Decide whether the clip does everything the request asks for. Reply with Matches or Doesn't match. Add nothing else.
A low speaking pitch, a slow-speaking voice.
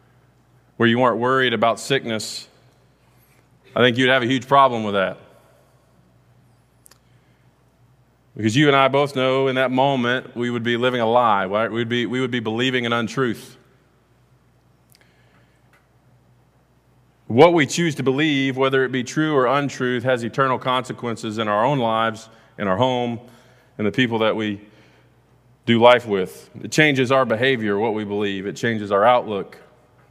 Doesn't match